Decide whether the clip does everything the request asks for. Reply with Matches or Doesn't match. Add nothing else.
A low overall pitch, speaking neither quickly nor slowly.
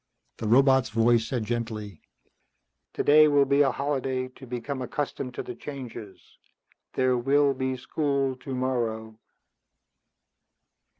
Doesn't match